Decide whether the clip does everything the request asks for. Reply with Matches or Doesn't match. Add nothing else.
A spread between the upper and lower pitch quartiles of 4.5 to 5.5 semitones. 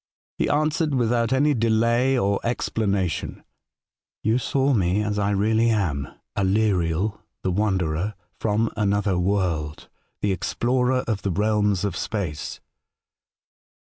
Doesn't match